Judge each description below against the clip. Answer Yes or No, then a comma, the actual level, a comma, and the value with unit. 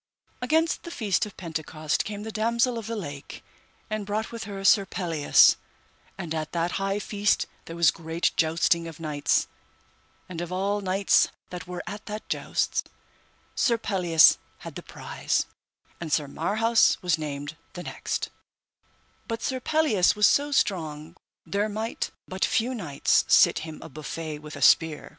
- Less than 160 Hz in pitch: No, medium, 185 Hz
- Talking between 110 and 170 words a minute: Yes, average, 160 wpm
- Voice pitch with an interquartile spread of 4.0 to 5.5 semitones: Yes, average, 5.0 semitones